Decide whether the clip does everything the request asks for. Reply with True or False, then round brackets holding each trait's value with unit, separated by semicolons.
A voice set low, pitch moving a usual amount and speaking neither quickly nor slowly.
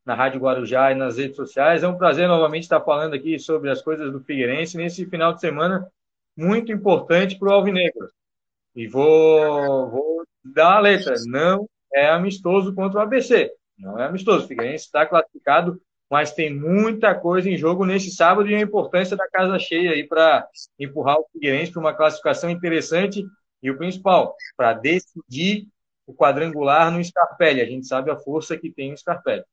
False (165 Hz; 4.3 semitones; 175 wpm)